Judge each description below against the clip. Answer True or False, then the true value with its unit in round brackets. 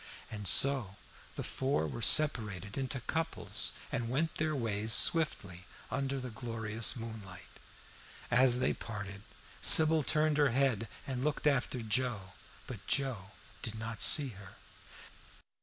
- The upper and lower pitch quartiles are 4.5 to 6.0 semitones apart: True (4.9 semitones)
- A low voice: True (120 Hz)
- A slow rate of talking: True (130 wpm)